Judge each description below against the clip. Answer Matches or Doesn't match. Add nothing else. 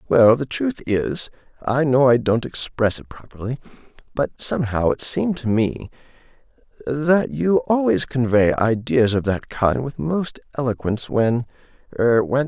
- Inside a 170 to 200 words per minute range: Doesn't match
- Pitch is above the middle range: Doesn't match